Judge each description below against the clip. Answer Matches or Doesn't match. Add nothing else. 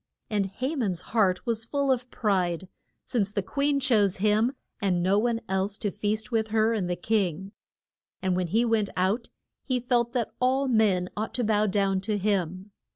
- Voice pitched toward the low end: Doesn't match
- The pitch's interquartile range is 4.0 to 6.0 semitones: Doesn't match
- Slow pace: Doesn't match